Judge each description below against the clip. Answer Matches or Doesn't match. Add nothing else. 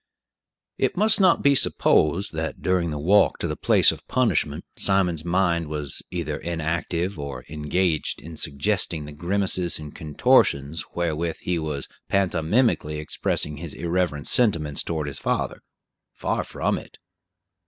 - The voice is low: Matches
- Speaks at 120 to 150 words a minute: Matches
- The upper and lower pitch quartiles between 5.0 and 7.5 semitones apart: Doesn't match